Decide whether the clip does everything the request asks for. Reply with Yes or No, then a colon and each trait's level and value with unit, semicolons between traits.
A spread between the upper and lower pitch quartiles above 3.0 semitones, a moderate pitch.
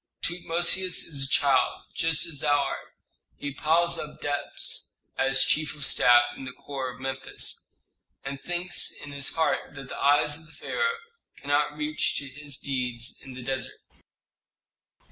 No: average, 2.7 semitones; medium, 145 Hz